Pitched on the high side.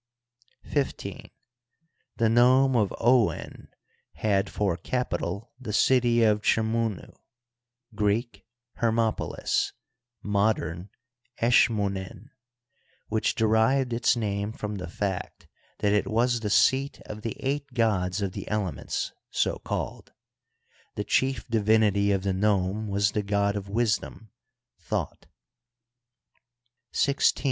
No: low, 105 Hz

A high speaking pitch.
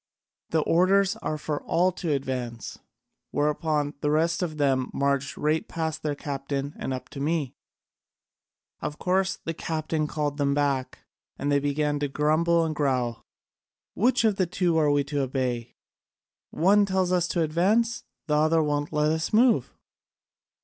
No: medium, 150 Hz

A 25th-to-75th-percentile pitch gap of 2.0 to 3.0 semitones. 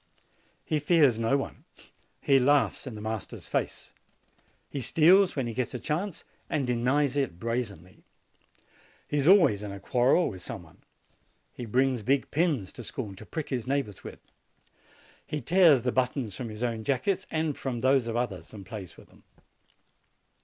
No: average, 4.6 semitones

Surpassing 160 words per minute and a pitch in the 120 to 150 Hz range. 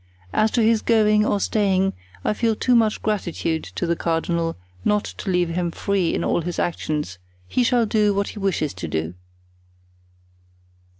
No: average, 170 wpm; high, 195 Hz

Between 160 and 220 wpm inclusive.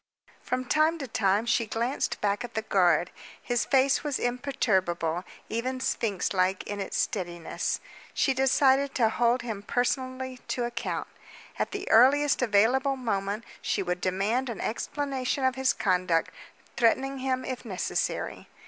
No: average, 145 wpm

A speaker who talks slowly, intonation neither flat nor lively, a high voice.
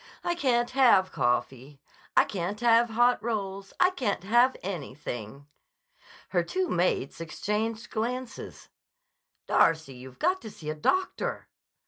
No: slow, 125 wpm; wide, 7.6 semitones; high, 205 Hz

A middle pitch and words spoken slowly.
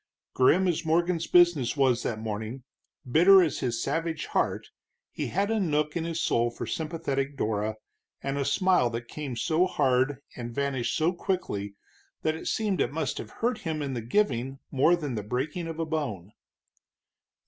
No: medium, 145 Hz; average, 175 wpm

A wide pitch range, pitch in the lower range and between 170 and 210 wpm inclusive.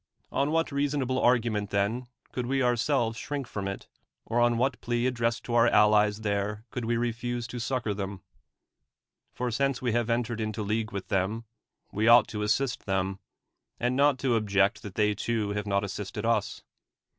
No: average, 2.8 semitones; low, 115 Hz; average, 180 wpm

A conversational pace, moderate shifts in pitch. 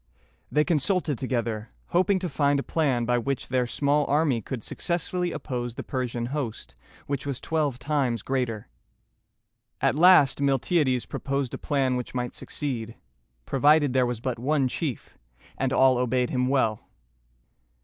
Yes: average, 150 wpm; average, 3.2 semitones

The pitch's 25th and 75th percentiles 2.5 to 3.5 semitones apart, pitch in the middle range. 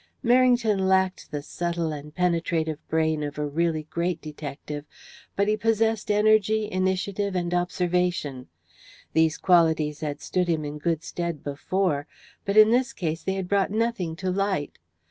No: average, 4.1 semitones; medium, 175 Hz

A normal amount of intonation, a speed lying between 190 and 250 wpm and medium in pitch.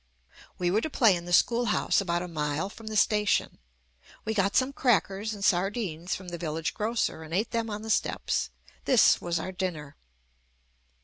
No: average, 4.1 semitones; average, 195 wpm; high, 195 Hz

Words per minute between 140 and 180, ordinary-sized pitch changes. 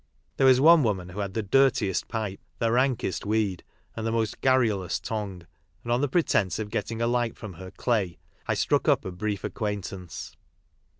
No: average, 190 wpm; average, 3.8 semitones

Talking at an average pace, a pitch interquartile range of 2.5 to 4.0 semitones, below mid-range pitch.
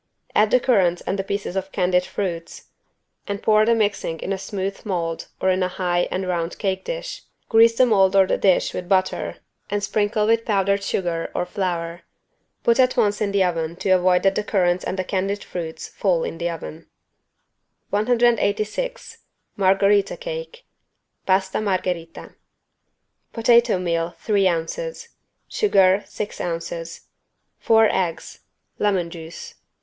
No: average, 150 wpm; average, 3.0 semitones; high, 195 Hz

